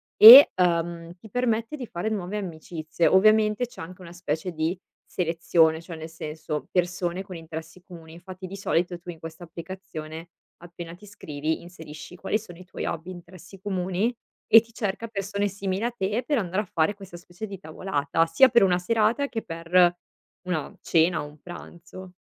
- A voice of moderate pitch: Yes, medium, 180 Hz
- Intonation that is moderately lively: Yes, average, 3.2 semitones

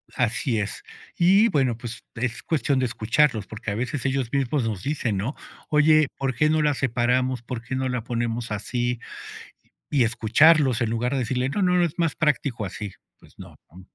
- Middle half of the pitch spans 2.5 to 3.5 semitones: No, average, 3.9 semitones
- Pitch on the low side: Yes, low, 125 Hz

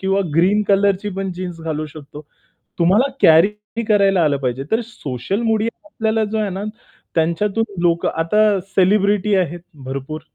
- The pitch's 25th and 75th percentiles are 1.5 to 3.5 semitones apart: No, average, 4.4 semitones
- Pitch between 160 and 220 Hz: Yes, high, 190 Hz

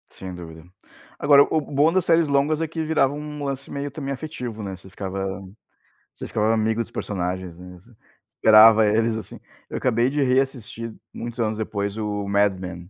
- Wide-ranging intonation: Yes, wide, 5.7 semitones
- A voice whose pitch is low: Yes, low, 115 Hz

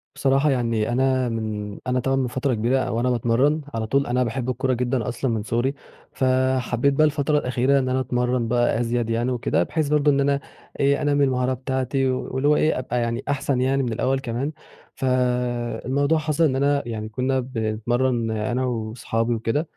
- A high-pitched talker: No, low, 125 Hz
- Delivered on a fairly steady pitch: Yes, narrow, 2.3 semitones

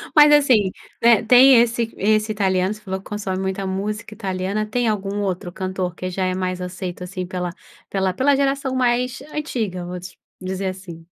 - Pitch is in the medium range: No, high, 195 Hz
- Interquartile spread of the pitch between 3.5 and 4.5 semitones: Yes, average, 3.9 semitones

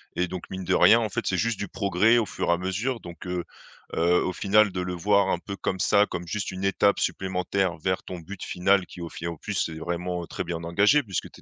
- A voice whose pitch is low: Yes, very low, 95 Hz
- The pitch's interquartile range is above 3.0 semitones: No, narrow, 2.4 semitones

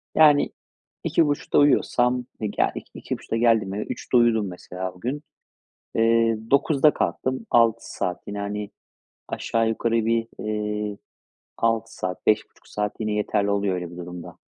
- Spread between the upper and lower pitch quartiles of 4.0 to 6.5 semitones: No, average, 2.7 semitones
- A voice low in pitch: Yes, low, 110 Hz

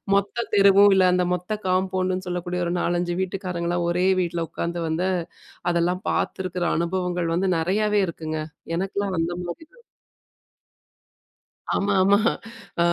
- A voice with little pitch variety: Yes, narrow, 1.8 semitones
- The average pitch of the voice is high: No, medium, 180 Hz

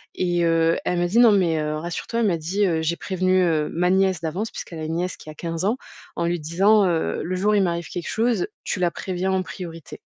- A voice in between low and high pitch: Yes, medium, 175 Hz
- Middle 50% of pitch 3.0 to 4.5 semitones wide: No, narrow, 2.5 semitones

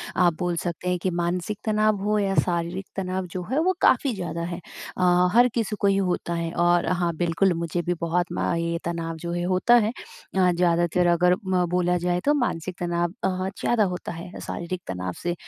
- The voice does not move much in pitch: Yes, narrow, 1.6 semitones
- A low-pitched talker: No, medium, 180 Hz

